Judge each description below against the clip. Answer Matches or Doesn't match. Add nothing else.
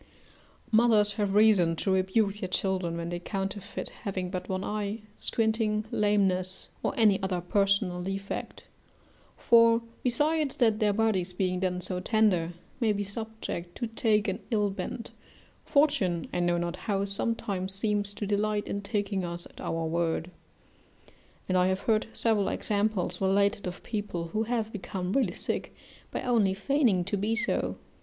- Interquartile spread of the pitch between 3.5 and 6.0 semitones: Doesn't match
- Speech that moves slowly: Doesn't match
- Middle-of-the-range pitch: Doesn't match